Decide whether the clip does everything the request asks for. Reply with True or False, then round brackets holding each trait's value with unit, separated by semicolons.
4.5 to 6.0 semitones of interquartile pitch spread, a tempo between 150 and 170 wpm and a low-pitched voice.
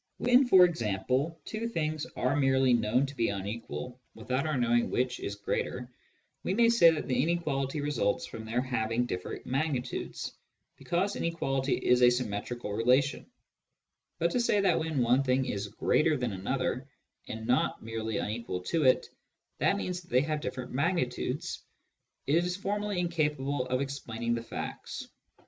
True (5.1 semitones; 155 wpm; 130 Hz)